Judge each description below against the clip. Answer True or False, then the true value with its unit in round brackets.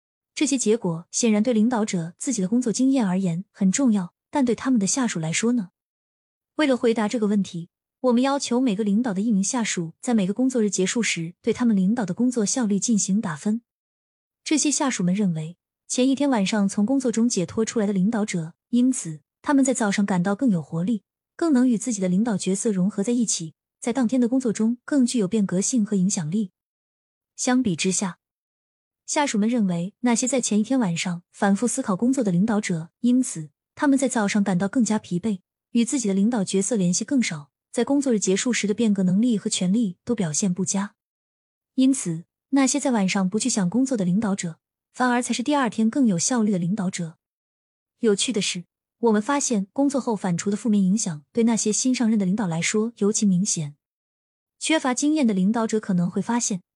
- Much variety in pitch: False (4.3 semitones)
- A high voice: True (215 Hz)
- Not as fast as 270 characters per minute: False (310 characters per minute)